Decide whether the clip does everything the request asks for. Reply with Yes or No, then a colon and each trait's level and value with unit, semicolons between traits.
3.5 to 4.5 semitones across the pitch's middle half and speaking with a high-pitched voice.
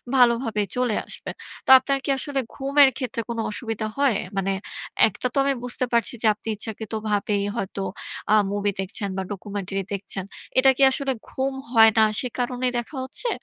Yes: average, 4.2 semitones; high, 230 Hz